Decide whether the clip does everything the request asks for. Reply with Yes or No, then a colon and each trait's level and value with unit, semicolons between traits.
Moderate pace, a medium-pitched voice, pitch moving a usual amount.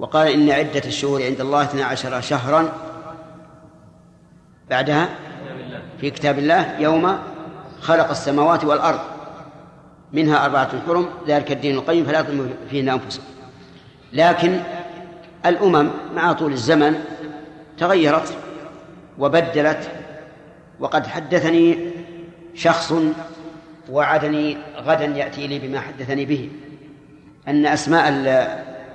No: average, 95 wpm; medium, 155 Hz; narrow, 2.3 semitones